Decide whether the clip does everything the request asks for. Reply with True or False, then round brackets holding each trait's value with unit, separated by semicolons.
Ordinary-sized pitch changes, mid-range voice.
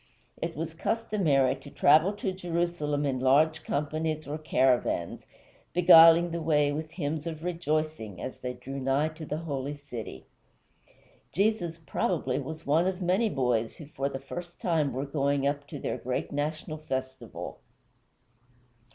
True (3.2 semitones; 155 Hz)